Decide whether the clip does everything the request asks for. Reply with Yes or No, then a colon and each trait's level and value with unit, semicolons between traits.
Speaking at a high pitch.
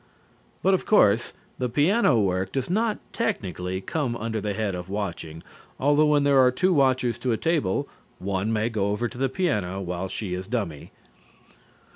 No: low, 115 Hz